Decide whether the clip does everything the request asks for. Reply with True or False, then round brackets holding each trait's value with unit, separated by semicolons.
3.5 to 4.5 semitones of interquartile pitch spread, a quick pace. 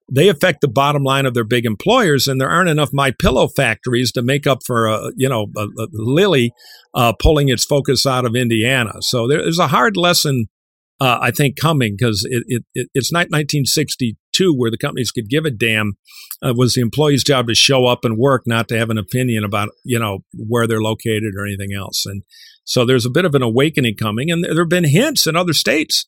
True (4.0 semitones; 220 wpm)